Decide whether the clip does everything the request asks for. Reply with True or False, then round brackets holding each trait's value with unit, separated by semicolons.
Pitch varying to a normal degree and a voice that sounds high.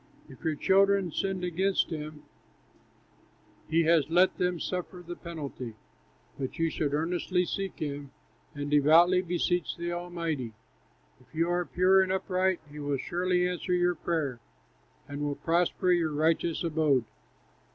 False (3.1 semitones; 170 Hz)